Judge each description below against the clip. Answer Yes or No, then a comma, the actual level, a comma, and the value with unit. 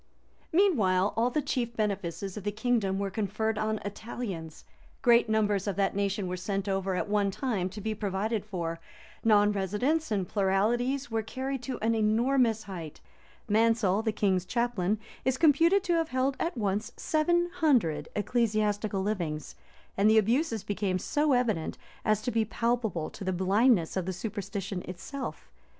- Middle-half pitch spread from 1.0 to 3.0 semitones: No, average, 3.8 semitones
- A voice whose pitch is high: Yes, high, 215 Hz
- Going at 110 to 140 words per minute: No, average, 160 wpm